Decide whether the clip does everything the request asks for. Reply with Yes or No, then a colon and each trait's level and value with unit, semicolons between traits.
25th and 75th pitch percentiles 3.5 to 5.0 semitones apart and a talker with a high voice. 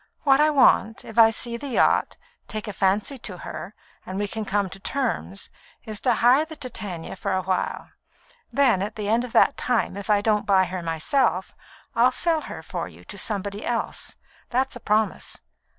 Yes: average, 4.2 semitones; high, 215 Hz